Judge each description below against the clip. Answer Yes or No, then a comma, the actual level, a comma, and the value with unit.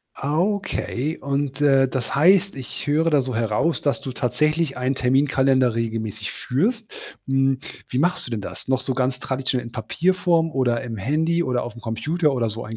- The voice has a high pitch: No, low, 135 Hz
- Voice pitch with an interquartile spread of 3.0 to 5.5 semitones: Yes, average, 4.0 semitones